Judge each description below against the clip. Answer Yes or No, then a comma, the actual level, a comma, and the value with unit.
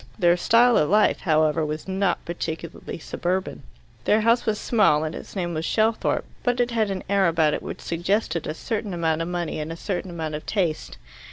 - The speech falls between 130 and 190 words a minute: No, average, 200 wpm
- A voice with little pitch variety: No, average, 4.8 semitones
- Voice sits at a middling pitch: Yes, medium, 175 Hz